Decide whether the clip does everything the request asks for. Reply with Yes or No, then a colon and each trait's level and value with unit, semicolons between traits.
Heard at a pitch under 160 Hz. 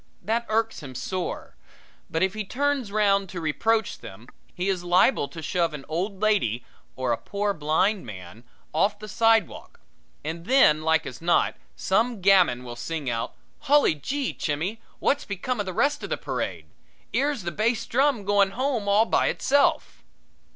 No: high, 195 Hz